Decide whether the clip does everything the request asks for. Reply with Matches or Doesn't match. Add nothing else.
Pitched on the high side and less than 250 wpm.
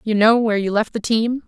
Doesn't match